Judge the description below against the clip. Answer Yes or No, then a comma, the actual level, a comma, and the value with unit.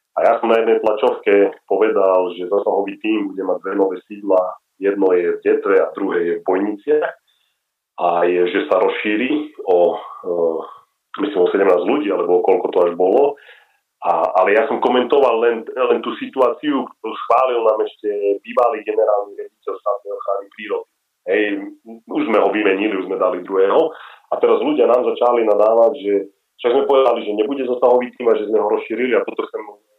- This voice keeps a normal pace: No, fast, 180 wpm